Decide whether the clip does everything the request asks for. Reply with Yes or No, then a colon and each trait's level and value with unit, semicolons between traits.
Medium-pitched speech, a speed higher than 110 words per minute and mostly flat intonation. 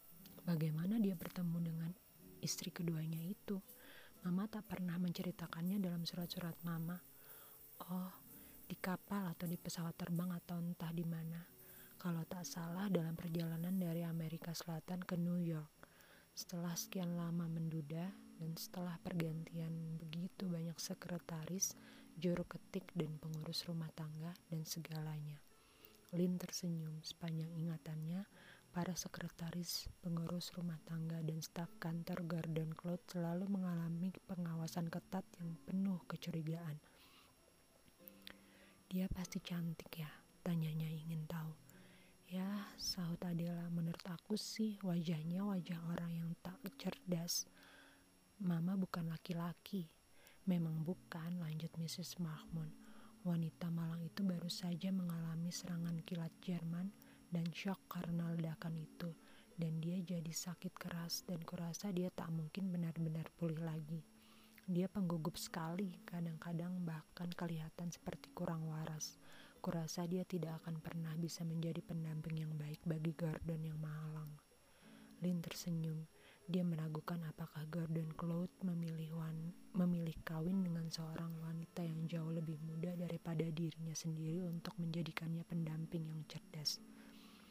Yes: medium, 170 Hz; average, 120 wpm; narrow, 1.7 semitones